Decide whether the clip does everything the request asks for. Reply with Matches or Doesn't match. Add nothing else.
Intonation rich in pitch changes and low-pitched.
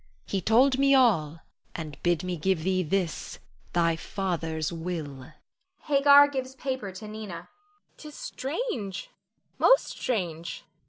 Doesn't match